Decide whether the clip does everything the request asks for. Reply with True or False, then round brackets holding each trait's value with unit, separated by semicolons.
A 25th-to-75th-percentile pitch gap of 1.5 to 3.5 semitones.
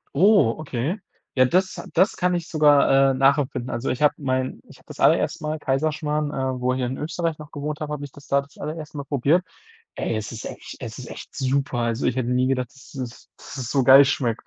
True (2.9 semitones)